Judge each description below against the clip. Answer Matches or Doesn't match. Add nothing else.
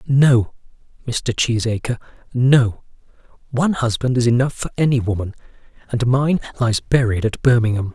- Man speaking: Matches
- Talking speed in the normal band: Doesn't match